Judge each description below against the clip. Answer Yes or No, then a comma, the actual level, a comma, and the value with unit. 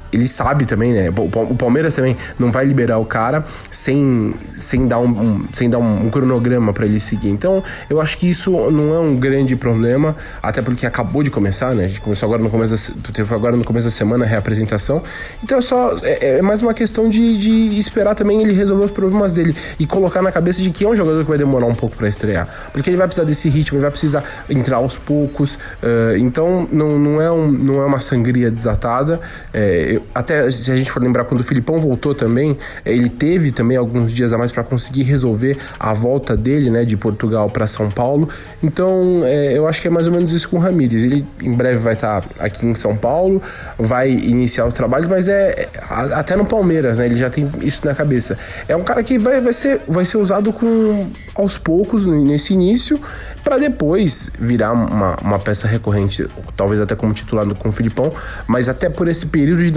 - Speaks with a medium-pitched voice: No, low, 130 Hz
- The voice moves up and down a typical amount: No, wide, 6.4 semitones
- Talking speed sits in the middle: No, fast, 215 wpm